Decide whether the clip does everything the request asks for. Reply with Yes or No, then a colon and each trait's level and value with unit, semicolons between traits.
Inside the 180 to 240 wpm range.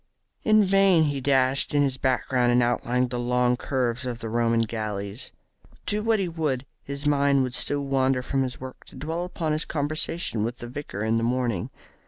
Yes: average, 195 wpm